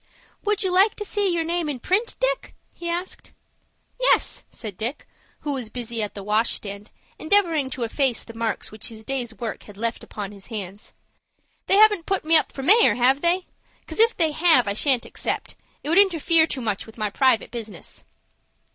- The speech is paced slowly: No, average, 195 wpm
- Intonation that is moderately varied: No, wide, 7.9 semitones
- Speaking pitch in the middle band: No, very high, 270 Hz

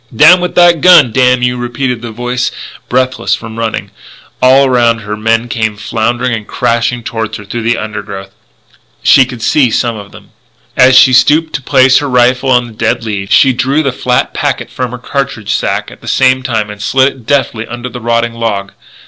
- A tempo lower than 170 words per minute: No, average, 200 wpm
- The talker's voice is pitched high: No, low, 120 Hz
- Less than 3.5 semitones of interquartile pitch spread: Yes, narrow, 2.4 semitones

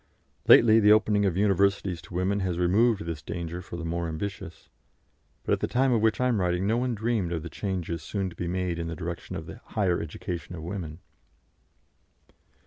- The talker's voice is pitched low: Yes, very low, 90 Hz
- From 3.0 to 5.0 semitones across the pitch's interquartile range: Yes, average, 3.3 semitones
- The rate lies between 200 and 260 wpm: Yes, fast, 205 wpm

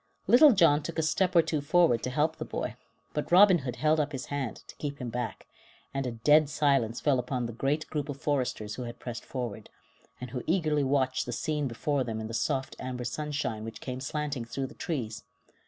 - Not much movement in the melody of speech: No, average, 3.7 semitones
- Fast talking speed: Yes, fast, 220 wpm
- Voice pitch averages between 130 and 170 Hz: Yes, medium, 140 Hz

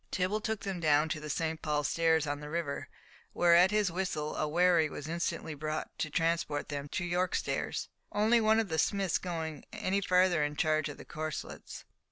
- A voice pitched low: No, medium, 165 Hz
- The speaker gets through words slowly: No, average, 200 wpm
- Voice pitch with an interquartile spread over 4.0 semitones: No, average, 3.3 semitones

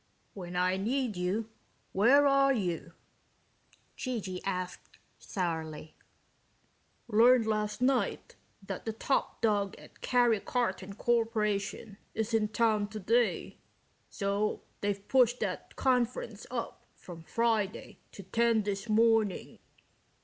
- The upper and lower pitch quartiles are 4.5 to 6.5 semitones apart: No, average, 3.1 semitones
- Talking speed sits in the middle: No, slow, 110 wpm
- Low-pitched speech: No, high, 215 Hz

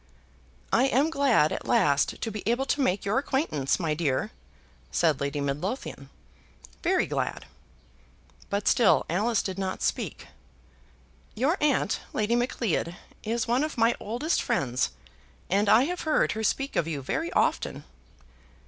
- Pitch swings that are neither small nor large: No, wide, 8.2 semitones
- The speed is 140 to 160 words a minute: Yes, average, 145 wpm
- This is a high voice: Yes, high, 220 Hz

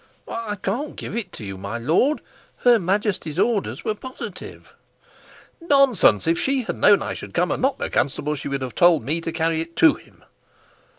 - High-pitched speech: No, medium, 180 Hz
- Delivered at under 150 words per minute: No, average, 185 wpm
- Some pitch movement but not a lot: No, wide, 7.9 semitones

